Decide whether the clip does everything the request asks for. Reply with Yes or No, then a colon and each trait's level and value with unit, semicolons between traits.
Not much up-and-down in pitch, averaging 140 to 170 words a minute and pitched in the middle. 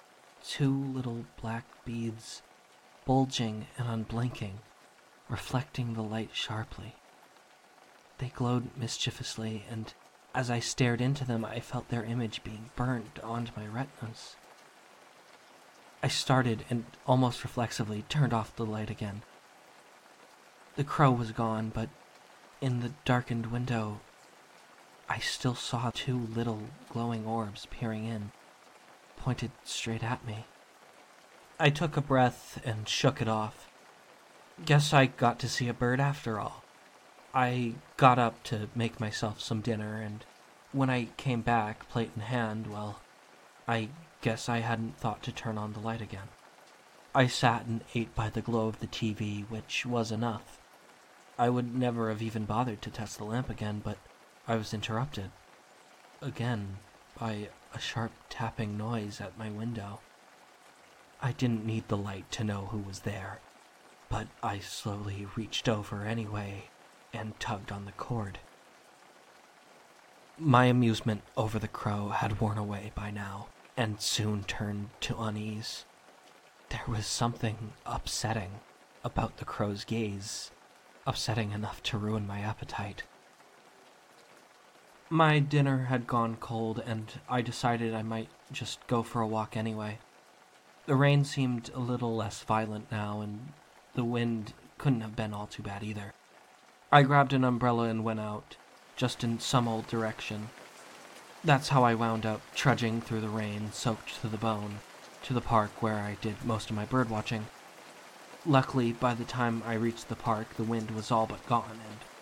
No: narrow, 2.3 semitones; average, 150 wpm; low, 115 Hz